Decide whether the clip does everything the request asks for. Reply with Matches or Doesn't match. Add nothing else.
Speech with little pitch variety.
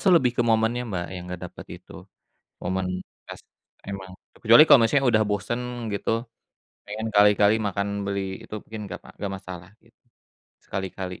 Doesn't match